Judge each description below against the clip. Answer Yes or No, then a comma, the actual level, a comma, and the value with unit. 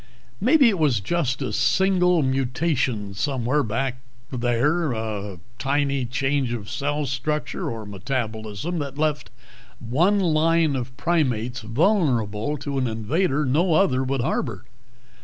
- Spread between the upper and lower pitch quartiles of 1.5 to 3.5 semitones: No, average, 4.6 semitones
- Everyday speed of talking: No, slow, 130 wpm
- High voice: No, low, 135 Hz